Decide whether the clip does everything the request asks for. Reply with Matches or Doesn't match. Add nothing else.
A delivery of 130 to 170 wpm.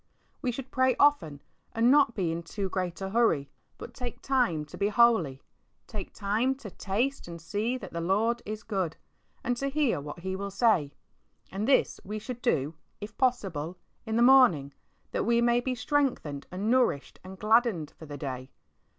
Doesn't match